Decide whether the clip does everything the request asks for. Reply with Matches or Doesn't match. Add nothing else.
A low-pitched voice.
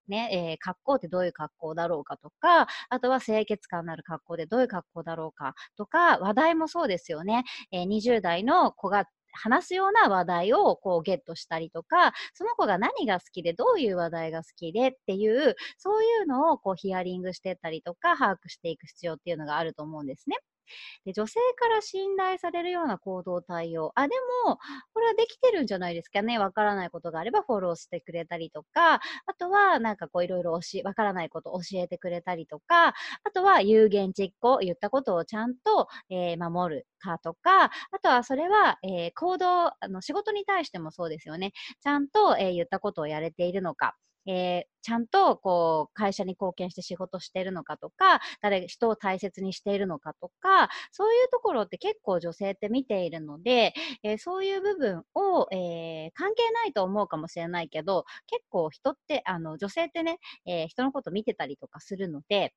Doesn't match